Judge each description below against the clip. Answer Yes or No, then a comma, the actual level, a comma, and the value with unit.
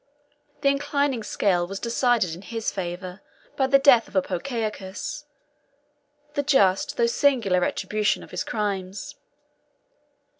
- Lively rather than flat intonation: Yes, wide, 6.1 semitones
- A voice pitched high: Yes, high, 220 Hz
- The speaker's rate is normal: No, slow, 120 wpm